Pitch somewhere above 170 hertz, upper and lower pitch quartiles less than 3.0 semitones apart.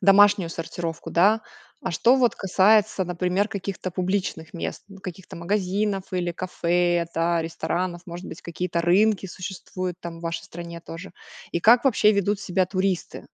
Yes: medium, 185 Hz; narrow, 2.6 semitones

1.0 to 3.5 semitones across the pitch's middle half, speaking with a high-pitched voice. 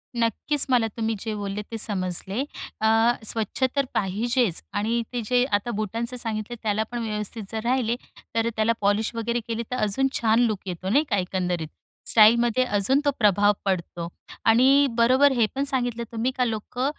Yes: average, 2.9 semitones; high, 225 Hz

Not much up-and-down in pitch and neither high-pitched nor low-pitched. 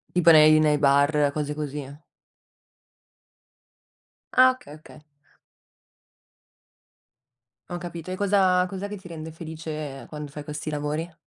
No: average, 3.0 semitones; medium, 155 Hz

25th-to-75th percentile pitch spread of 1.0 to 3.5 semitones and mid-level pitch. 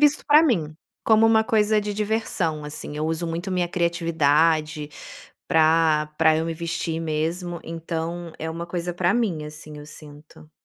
Yes: average, 2.7 semitones; medium, 165 Hz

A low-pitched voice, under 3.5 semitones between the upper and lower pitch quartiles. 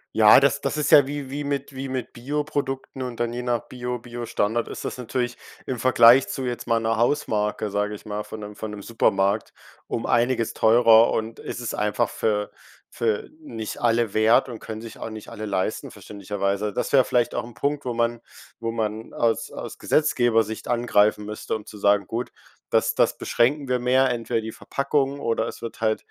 Yes: low, 115 Hz; average, 2.8 semitones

